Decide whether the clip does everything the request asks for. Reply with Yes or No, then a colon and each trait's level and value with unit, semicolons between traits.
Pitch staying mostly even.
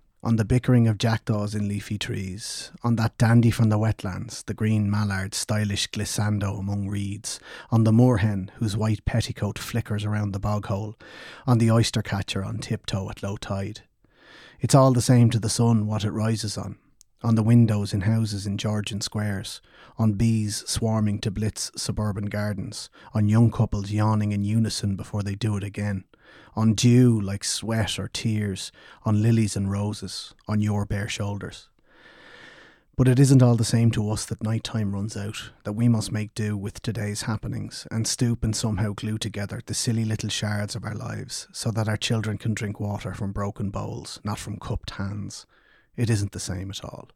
Yes: narrow, 1.8 semitones